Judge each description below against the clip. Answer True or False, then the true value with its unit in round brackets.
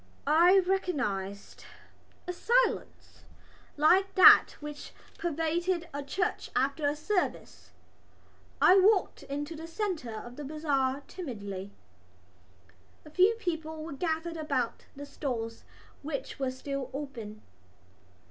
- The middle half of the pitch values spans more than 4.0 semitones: True (4.7 semitones)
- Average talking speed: False (110 wpm)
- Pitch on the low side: False (300 Hz)